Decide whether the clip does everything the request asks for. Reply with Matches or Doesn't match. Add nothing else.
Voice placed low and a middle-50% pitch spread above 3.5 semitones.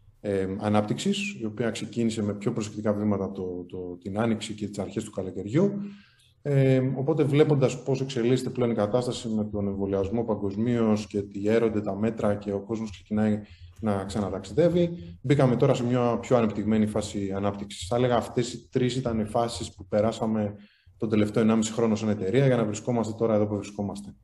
Doesn't match